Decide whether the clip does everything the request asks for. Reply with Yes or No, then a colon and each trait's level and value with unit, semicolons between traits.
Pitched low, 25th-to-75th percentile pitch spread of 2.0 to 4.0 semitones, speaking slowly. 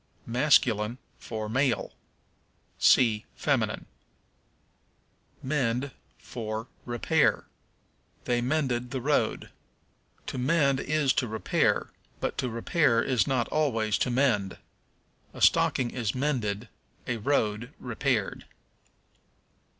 Yes: low, 125 Hz; average, 3.5 semitones; slow, 95 wpm